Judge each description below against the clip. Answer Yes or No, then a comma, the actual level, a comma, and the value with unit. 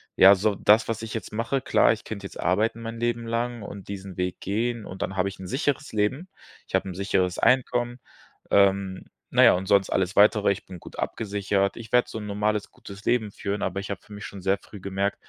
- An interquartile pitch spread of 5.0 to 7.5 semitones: No, average, 2.7 semitones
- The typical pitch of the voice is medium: No, low, 100 Hz